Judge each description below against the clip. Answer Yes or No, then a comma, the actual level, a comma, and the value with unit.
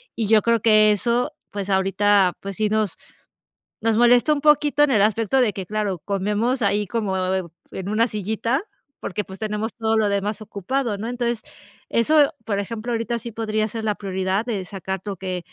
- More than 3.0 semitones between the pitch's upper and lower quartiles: No, average, 2.7 semitones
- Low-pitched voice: No, high, 215 Hz